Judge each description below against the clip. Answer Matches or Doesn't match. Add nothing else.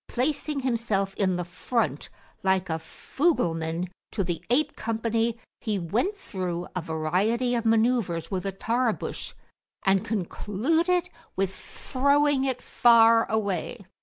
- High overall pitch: Matches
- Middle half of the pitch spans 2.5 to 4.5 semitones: Doesn't match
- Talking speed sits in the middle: Doesn't match